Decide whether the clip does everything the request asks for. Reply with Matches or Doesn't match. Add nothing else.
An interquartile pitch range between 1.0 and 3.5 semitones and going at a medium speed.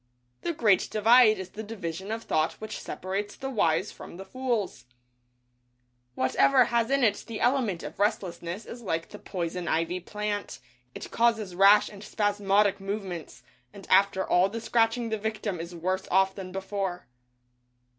Matches